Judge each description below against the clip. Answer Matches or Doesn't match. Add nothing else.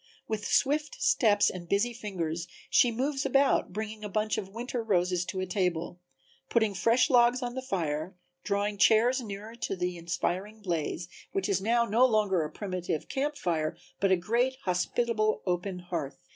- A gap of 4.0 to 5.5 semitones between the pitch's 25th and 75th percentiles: Matches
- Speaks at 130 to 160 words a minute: Doesn't match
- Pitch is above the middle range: Matches